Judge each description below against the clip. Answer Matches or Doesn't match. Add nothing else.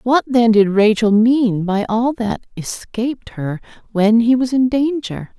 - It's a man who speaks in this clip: Doesn't match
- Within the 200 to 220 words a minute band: Doesn't match